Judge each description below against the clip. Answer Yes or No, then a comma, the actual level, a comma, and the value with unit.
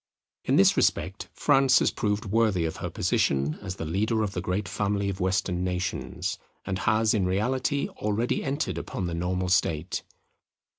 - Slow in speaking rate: No, average, 165 wpm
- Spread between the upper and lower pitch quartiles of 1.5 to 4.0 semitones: Yes, average, 3.1 semitones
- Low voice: Yes, very low, 95 Hz